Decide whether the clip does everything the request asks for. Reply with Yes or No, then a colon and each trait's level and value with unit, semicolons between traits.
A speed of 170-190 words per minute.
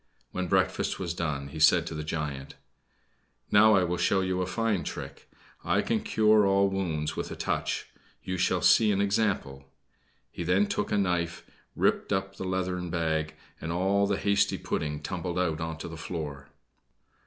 Yes: average, 175 wpm